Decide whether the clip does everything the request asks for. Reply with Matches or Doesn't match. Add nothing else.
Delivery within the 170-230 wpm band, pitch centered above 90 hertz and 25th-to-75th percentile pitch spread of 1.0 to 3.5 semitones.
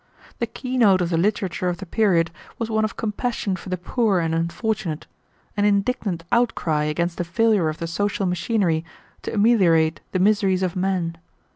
Doesn't match